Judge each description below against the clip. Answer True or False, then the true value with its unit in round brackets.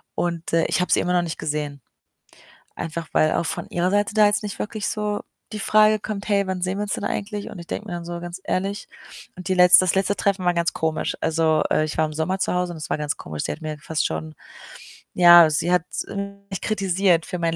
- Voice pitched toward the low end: False (180 Hz)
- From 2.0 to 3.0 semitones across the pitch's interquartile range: False (3.6 semitones)